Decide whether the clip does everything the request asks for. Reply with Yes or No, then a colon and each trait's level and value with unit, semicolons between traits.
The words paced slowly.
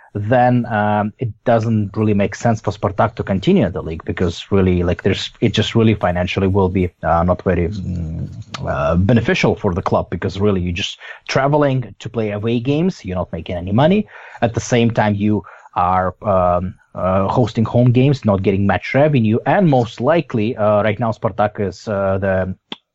No: average, 185 wpm